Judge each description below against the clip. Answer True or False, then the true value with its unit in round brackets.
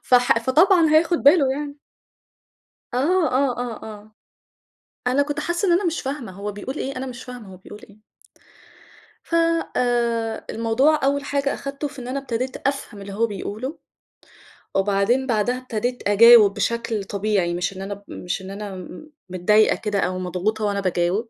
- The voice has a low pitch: False (235 Hz)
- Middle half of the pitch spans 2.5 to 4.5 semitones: False (5.2 semitones)